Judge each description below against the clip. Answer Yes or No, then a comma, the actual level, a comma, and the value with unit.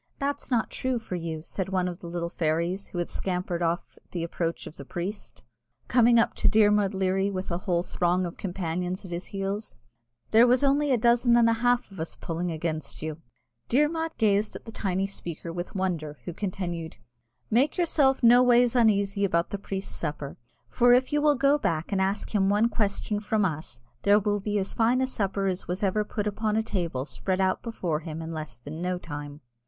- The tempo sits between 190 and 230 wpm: Yes, fast, 205 wpm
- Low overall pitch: No, high, 195 Hz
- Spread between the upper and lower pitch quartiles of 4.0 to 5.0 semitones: Yes, average, 4.7 semitones